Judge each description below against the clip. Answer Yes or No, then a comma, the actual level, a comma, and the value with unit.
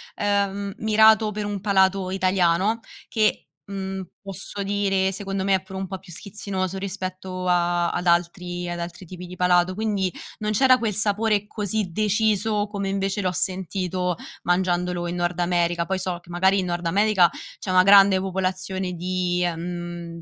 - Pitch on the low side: No, high, 190 Hz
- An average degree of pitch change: No, narrow, 2.1 semitones